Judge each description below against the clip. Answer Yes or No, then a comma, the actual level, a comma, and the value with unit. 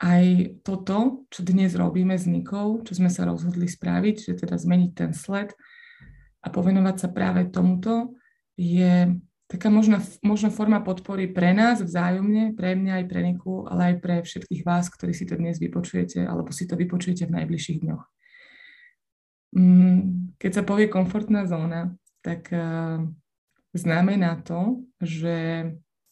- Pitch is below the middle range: No, medium, 180 Hz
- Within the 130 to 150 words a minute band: Yes, average, 140 wpm